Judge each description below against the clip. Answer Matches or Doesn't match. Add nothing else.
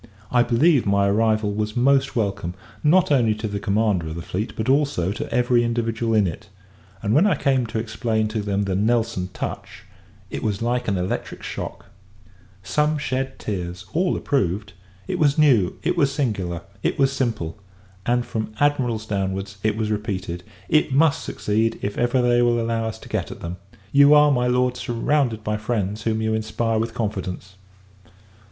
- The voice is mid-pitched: Doesn't match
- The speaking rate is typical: Matches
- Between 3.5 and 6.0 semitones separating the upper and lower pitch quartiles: Matches